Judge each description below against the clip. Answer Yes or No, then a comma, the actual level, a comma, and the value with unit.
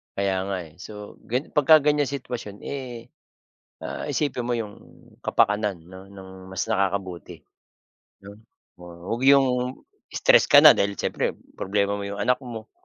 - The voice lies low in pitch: Yes, low, 105 Hz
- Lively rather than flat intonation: No, average, 4.4 semitones